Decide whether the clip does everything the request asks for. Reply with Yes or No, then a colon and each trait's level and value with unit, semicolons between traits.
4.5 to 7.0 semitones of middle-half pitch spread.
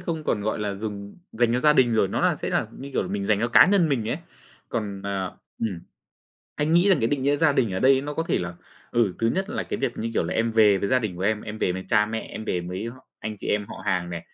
Yes: average, 5.0 semitones